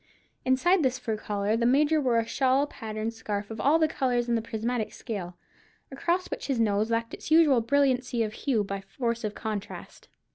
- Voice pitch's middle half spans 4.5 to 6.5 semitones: No, average, 3.7 semitones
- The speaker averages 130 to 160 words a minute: No, average, 190 wpm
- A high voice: Yes, high, 235 Hz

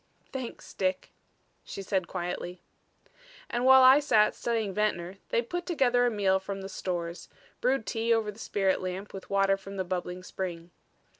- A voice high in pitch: Yes, high, 195 Hz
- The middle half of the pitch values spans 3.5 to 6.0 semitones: Yes, average, 3.9 semitones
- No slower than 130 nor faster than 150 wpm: No, average, 165 wpm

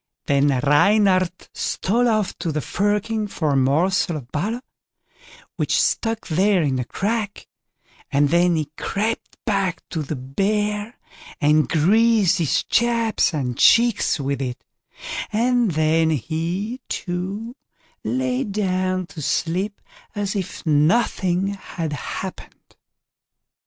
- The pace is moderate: No, slow, 120 wpm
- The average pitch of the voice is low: No, medium, 185 Hz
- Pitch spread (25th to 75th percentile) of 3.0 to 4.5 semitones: No, wide, 5.4 semitones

